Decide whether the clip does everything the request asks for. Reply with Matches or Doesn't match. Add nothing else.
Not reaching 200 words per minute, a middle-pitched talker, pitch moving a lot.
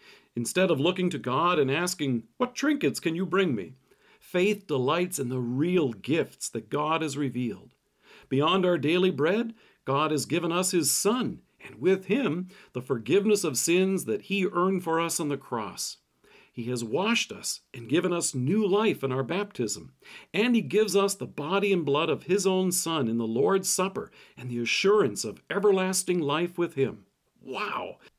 Matches